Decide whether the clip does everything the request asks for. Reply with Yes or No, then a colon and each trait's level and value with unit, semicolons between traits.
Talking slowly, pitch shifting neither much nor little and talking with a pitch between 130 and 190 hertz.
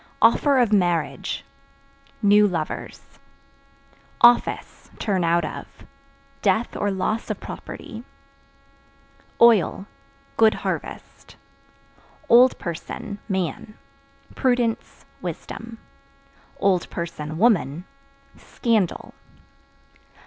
No: slow, 70 wpm; average, 5.0 semitones; high, 205 Hz